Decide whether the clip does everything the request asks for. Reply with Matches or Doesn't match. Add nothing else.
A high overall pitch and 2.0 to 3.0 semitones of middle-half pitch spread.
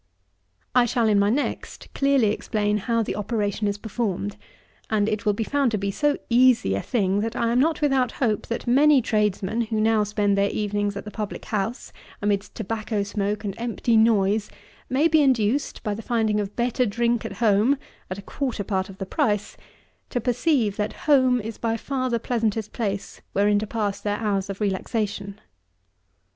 Matches